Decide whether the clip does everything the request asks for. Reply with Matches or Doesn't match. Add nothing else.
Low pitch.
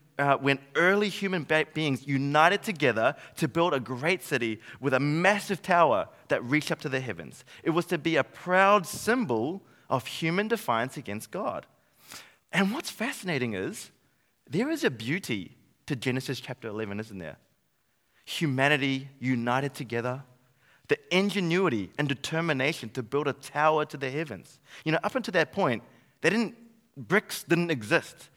Doesn't match